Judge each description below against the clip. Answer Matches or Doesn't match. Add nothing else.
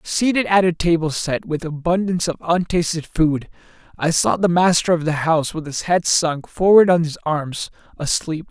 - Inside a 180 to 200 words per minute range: Matches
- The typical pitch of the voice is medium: Matches